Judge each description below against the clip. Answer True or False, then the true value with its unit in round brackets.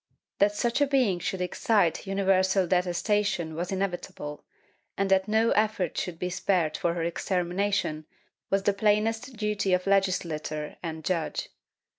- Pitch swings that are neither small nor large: True (3.0 semitones)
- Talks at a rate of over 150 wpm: False (140 wpm)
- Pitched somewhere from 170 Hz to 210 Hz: True (190 Hz)